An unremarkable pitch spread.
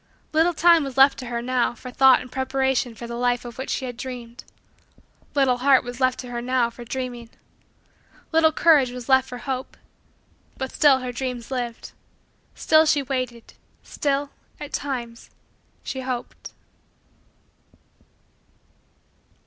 No: narrow, 1.9 semitones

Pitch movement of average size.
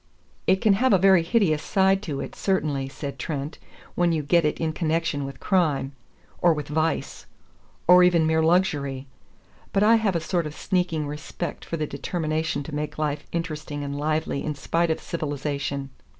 Yes: average, 3.3 semitones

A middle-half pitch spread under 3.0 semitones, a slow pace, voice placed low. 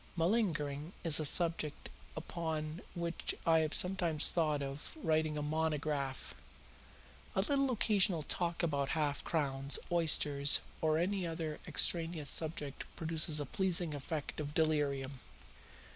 No: narrow, 2.5 semitones; slow, 125 wpm; medium, 155 Hz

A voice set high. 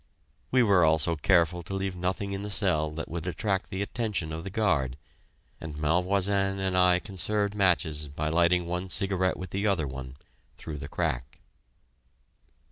No: very low, 90 Hz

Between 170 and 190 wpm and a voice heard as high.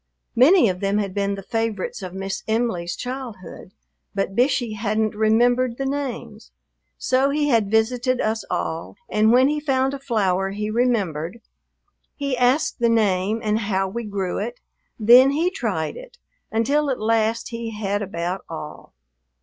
No: average, 155 wpm; high, 225 Hz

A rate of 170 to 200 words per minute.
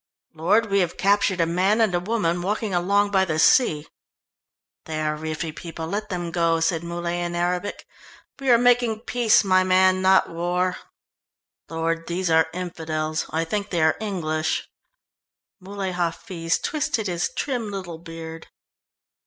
No: average, 155 wpm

